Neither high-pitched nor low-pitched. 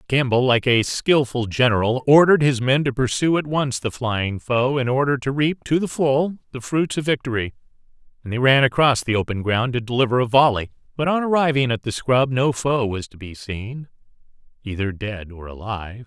No: low, 125 Hz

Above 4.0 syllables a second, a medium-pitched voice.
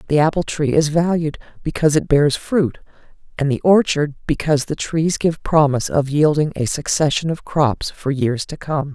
Yes: 5.0 syllables/s; medium, 150 Hz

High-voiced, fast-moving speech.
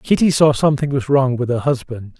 No: low, 135 Hz; fast, 220 wpm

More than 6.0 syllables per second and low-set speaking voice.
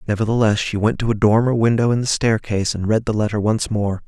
Yes: 6.2 syllables/s; low, 110 Hz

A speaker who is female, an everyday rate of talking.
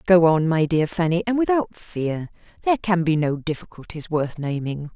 Yes: female; average, 180 wpm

